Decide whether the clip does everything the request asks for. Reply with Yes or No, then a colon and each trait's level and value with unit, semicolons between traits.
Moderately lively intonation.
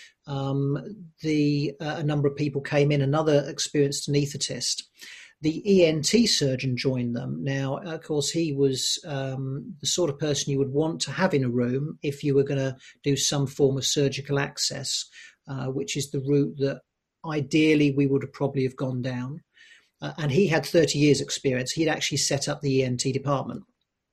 No: narrow, 1.9 semitones